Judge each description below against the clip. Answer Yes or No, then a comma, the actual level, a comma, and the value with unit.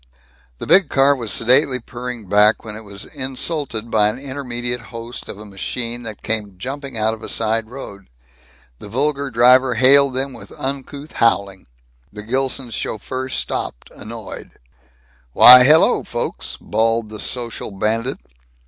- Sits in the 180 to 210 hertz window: No, low, 120 Hz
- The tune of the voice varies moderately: Yes, average, 3.4 semitones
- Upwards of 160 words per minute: No, average, 150 wpm